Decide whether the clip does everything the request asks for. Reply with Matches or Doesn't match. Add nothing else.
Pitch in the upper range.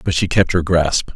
Doesn't match